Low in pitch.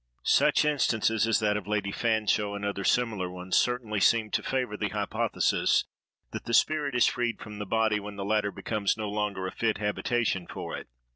Yes: low, 105 Hz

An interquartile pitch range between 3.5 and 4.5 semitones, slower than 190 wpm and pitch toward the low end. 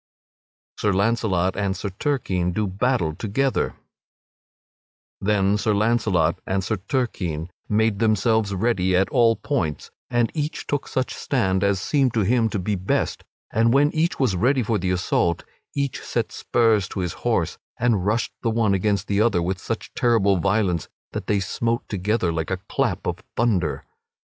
Yes: average, 3.9 semitones; average, 165 wpm; low, 105 Hz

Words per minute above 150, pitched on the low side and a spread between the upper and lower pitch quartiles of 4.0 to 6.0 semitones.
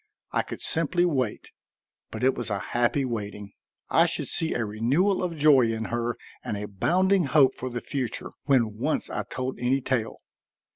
Yes: average, 180 wpm; low, 130 Hz; average, 5.2 semitones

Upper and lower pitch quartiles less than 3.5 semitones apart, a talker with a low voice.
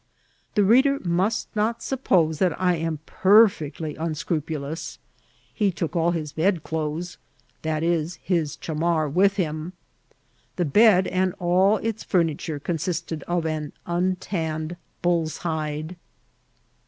No: average, 2.9 semitones; medium, 170 Hz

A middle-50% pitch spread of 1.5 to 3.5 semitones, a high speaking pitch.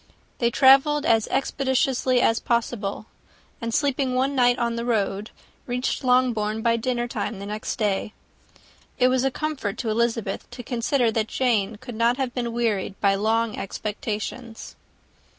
Yes: average, 2.8 semitones; high, 235 Hz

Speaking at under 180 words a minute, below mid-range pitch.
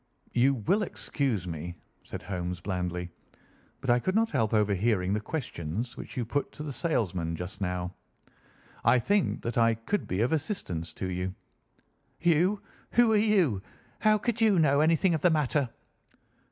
Yes: average, 165 wpm; low, 120 Hz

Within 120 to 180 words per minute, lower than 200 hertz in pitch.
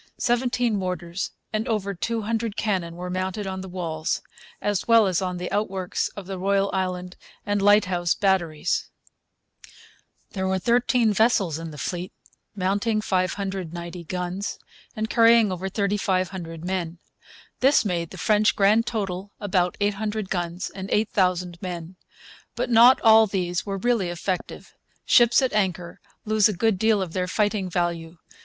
Yes: average, 150 wpm; high, 190 Hz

